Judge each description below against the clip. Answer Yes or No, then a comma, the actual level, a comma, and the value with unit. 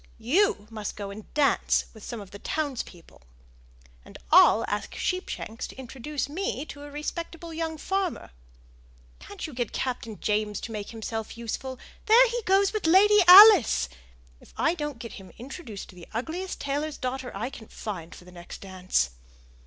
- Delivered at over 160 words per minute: Yes, average, 170 wpm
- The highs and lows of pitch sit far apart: Yes, wide, 7.4 semitones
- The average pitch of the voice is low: No, very high, 260 Hz